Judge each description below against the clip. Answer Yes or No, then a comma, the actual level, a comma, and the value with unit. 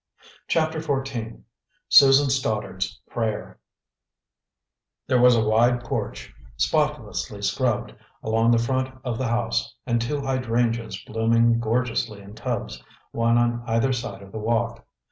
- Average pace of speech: No, slow, 125 wpm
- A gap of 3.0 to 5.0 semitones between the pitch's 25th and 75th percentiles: No, narrow, 2.5 semitones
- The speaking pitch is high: No, low, 115 Hz